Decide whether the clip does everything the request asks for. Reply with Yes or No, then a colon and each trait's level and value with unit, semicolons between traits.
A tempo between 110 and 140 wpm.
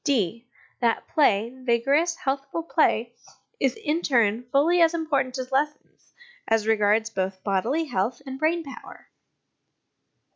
Yes: slow, 135 wpm